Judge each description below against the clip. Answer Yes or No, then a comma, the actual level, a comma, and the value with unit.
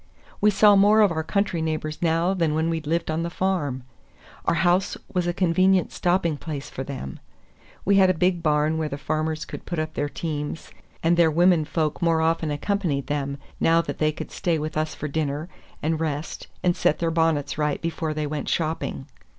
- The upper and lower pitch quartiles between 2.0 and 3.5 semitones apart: Yes, narrow, 2.4 semitones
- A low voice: No, medium, 160 Hz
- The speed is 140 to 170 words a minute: No, average, 200 wpm